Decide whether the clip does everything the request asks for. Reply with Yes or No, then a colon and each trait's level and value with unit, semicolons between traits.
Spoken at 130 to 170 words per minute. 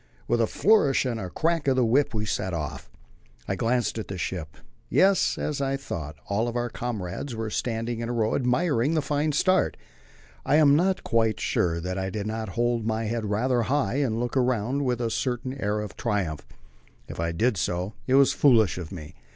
No: average, 200 wpm